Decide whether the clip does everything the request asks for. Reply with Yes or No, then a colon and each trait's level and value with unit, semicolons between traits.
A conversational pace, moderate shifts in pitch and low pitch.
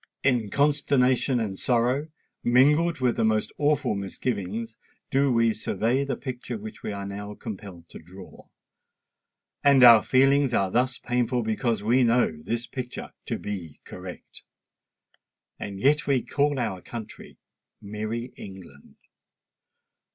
No: slow, 130 wpm; average, 4.0 semitones; low, 120 Hz